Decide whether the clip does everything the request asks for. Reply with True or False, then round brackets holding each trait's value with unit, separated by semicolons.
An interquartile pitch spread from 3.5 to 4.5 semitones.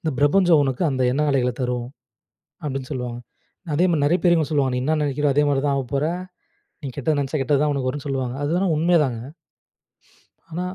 False (2.8 semitones)